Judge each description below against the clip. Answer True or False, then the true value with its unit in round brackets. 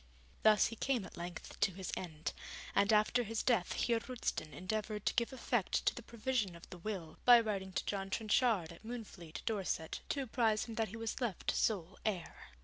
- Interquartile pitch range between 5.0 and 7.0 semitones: False (3.7 semitones)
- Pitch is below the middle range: False (215 Hz)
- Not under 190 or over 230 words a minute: True (195 wpm)